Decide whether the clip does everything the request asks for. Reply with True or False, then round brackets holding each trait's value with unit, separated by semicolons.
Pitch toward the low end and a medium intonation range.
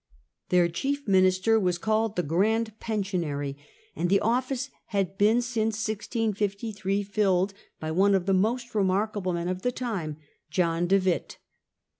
False (200 Hz; 3.4 semitones)